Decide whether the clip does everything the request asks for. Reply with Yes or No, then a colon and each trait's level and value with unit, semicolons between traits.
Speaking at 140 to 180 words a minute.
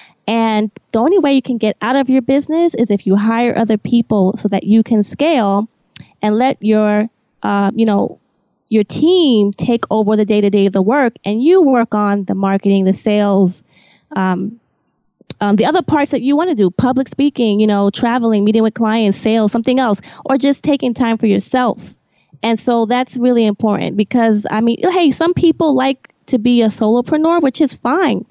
No: average, 195 wpm